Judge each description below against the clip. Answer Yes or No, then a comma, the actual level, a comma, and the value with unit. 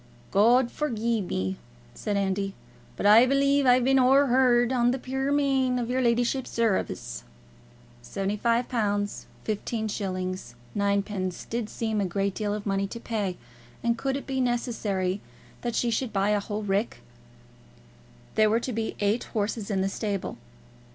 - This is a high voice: Yes, high, 220 Hz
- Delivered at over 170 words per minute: No, average, 150 wpm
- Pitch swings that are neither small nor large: Yes, average, 3.7 semitones